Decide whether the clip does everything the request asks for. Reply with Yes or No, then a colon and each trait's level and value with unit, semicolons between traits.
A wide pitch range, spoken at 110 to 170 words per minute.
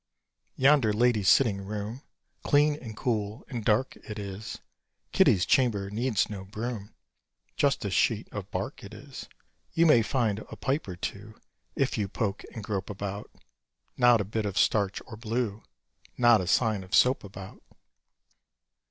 No: average, 3.3 semitones; average, 155 wpm